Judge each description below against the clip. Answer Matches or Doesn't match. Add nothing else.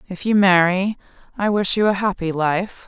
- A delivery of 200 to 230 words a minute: Doesn't match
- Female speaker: Matches